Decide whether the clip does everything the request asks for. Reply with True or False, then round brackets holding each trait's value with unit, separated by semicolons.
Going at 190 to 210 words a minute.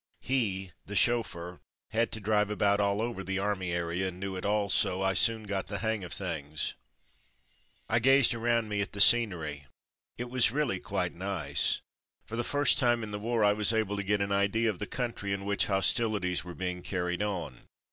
True (200 wpm)